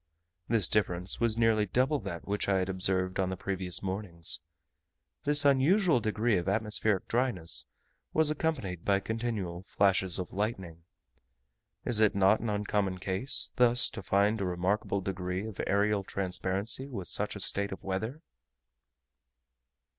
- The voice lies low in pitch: Yes, low, 100 Hz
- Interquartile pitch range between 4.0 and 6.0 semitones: No, average, 3.4 semitones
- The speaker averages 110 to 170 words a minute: Yes, average, 145 wpm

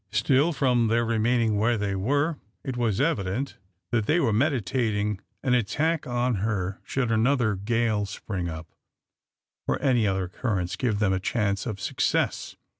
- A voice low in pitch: Yes, low, 115 Hz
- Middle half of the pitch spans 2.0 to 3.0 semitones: No, average, 3.8 semitones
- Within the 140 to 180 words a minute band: Yes, average, 155 wpm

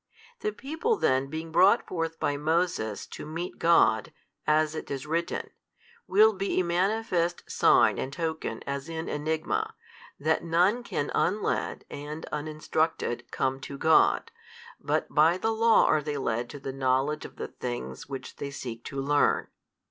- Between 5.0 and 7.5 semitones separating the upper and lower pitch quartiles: No, average, 3.8 semitones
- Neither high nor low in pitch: Yes, medium, 155 Hz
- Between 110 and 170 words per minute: Yes, average, 160 wpm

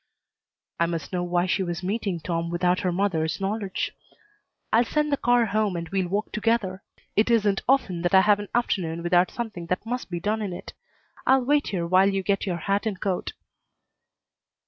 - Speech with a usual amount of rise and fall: Yes, average, 3.6 semitones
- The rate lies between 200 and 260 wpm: No, average, 190 wpm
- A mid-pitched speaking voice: No, high, 195 Hz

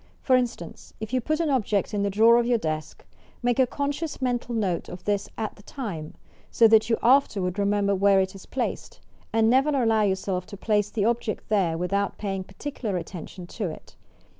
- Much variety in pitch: No, average, 3.9 semitones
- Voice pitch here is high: Yes, high, 210 Hz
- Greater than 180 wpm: Yes, average, 195 wpm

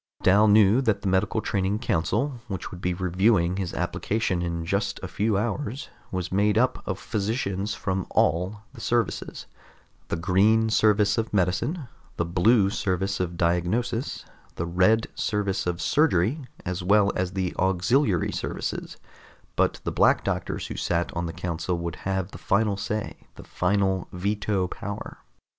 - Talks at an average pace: Yes, average, 155 wpm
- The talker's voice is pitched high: No, very low, 95 Hz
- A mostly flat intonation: No, average, 3.2 semitones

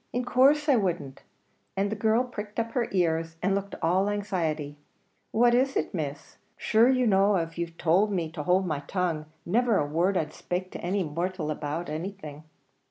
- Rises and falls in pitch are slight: No, average, 4.7 semitones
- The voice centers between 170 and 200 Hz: Yes, medium, 185 Hz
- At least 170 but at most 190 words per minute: Yes, average, 185 wpm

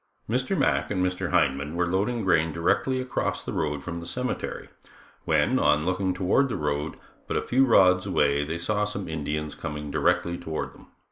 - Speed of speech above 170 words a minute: Yes, average, 185 wpm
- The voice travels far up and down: No, average, 4.3 semitones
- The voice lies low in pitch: Yes, very low, 85 Hz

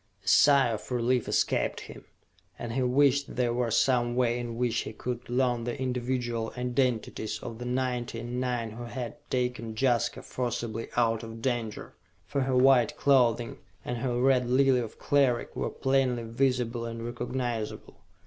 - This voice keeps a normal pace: Yes, average, 160 wpm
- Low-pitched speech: Yes, low, 120 Hz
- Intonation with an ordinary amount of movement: No, narrow, 1.6 semitones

